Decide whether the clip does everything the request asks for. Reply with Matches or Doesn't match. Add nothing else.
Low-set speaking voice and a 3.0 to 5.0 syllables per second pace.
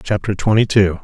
Doesn't match